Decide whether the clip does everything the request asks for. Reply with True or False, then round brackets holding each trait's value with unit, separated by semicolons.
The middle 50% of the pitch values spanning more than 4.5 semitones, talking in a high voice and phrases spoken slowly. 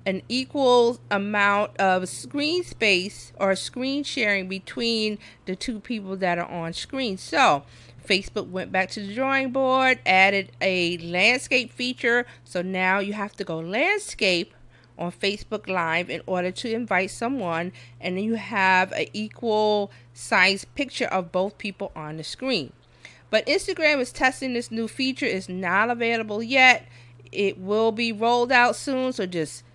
False (4.9 semitones; 205 Hz; 155 wpm)